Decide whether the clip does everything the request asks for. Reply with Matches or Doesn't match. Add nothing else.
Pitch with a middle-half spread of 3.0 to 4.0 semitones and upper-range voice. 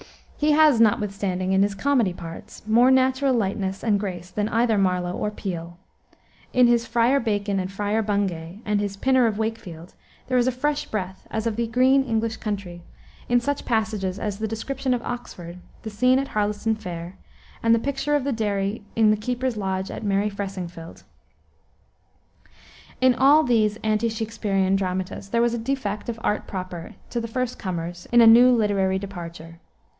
Matches